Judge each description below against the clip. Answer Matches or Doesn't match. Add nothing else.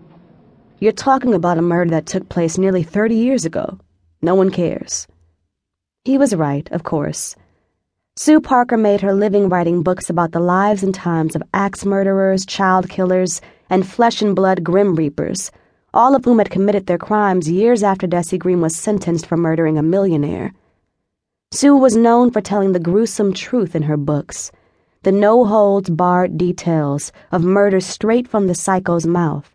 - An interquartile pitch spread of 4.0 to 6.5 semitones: Doesn't match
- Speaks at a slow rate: Doesn't match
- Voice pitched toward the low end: Doesn't match